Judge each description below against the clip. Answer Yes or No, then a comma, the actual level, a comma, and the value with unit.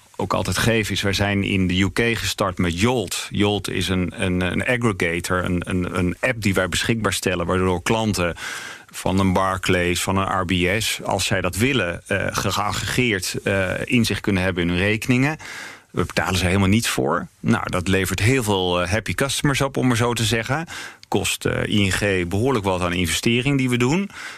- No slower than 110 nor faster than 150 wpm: No, average, 180 wpm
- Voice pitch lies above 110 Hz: No, low, 100 Hz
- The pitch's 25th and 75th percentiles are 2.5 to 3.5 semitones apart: No, average, 4.0 semitones